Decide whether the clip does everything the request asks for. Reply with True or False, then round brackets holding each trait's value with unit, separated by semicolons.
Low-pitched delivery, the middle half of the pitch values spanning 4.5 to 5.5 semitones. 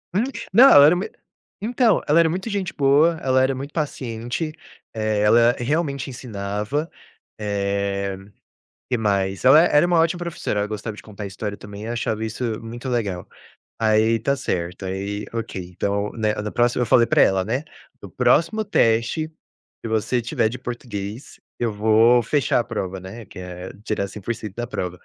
True (115 Hz; 5.1 semitones)